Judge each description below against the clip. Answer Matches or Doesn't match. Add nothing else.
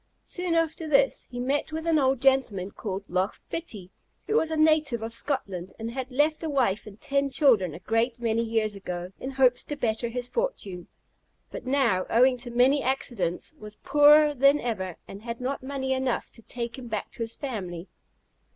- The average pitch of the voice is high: Matches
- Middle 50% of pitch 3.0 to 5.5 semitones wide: Matches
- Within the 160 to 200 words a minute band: Matches